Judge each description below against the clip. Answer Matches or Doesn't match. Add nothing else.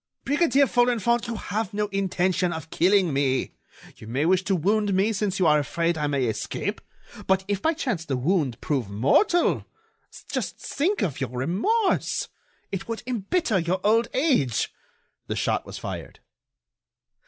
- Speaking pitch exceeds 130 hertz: Matches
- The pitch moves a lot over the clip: Matches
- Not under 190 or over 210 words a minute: Doesn't match